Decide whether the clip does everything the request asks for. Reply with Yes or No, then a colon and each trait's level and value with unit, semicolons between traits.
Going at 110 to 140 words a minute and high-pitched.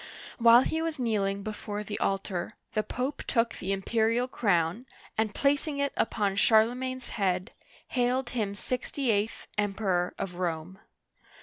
Yes: slow, 135 wpm; high, 220 Hz